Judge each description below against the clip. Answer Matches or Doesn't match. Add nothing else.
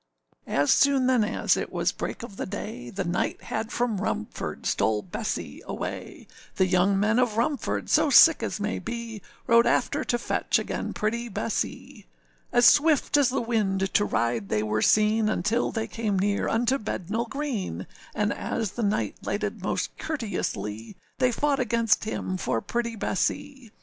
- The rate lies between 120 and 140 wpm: Doesn't match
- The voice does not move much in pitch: Doesn't match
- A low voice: Doesn't match